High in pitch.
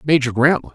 No: medium, 140 Hz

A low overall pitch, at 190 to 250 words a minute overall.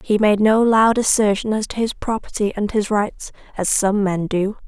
No: high, 210 Hz; fast, 205 wpm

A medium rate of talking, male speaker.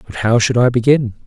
No: fast, 235 wpm; male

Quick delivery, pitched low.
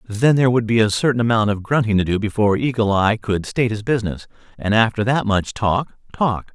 Yes: fast, 220 wpm; low, 110 Hz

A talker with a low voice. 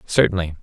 Yes: very low, 85 Hz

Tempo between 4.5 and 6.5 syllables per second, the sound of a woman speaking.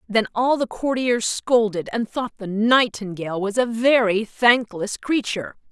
No: 4.3 syllables/s; female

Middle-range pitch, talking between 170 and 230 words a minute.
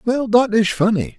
No: high, 215 Hz; fast, 205 wpm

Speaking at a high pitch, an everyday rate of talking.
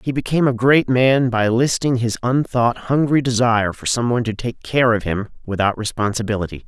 No: low, 120 Hz; average, 180 wpm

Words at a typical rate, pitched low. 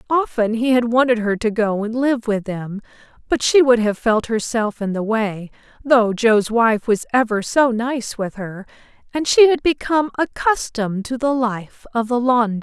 No: average, 190 wpm; high, 235 Hz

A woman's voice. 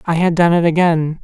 No: male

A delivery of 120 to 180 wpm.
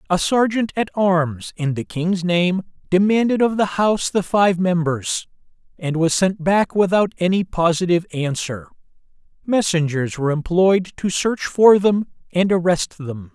Yes: average, 150 wpm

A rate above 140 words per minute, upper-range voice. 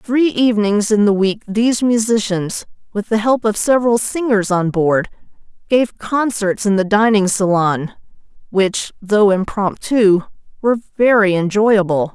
No: slow, 135 wpm; high, 210 Hz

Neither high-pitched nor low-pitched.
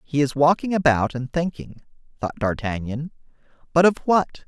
Yes: medium, 145 Hz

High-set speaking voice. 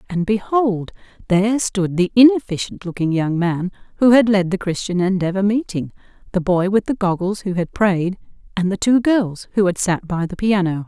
Yes: high, 195 Hz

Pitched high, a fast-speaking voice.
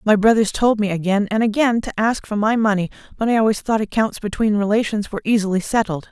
Yes: high, 215 Hz; fast, 215 wpm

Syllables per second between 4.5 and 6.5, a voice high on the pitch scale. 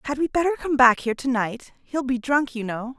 Yes: 5.5 syllables/s; very high, 260 Hz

